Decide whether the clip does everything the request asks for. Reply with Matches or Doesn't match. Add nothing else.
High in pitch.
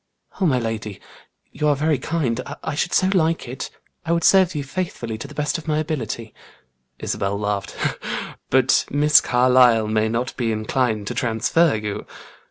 Doesn't match